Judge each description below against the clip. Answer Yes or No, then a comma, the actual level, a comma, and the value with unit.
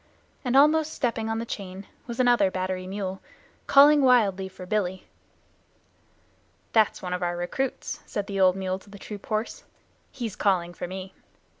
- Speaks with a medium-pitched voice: No, high, 200 Hz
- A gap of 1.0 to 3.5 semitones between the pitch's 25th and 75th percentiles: No, average, 4.1 semitones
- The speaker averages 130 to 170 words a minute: Yes, average, 160 wpm